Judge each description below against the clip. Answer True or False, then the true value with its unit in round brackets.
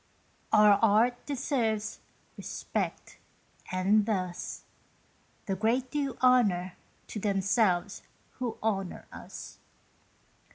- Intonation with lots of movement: False (3.8 semitones)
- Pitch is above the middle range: True (215 Hz)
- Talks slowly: True (85 wpm)